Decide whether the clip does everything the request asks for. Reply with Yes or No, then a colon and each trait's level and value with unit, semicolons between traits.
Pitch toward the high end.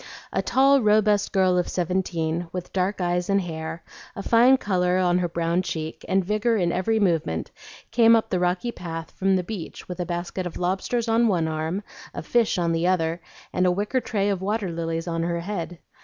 No: medium, 180 Hz